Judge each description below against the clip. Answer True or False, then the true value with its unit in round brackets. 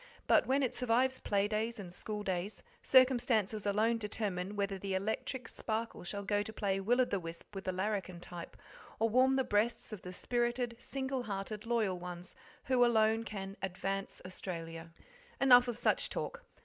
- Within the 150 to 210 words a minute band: True (175 wpm)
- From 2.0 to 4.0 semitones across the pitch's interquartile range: True (3.7 semitones)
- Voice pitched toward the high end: True (210 Hz)